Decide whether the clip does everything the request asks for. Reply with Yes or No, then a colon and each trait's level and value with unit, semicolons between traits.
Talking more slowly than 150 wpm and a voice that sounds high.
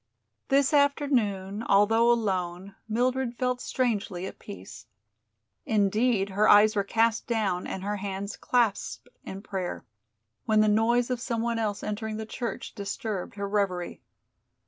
Yes: average, 140 wpm; high, 215 Hz